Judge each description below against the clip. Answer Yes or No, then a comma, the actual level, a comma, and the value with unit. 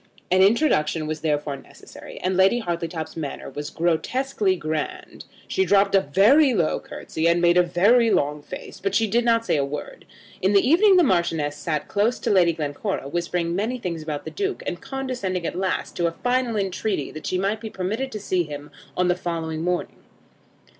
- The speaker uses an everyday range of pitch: No, wide, 5.7 semitones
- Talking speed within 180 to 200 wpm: Yes, average, 195 wpm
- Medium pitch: Yes, medium, 180 Hz